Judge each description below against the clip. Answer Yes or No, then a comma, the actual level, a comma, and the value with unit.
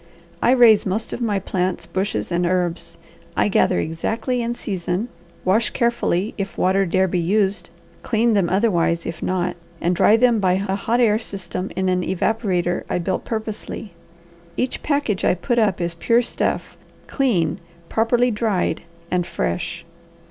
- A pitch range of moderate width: Yes, average, 4.1 semitones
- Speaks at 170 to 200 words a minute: No, average, 155 wpm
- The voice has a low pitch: No, high, 195 Hz